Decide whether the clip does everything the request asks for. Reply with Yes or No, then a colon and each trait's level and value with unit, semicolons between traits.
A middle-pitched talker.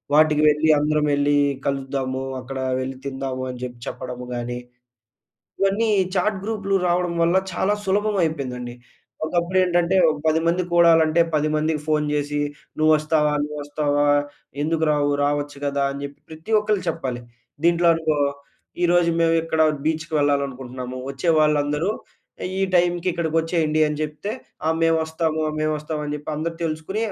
Yes: medium, 155 Hz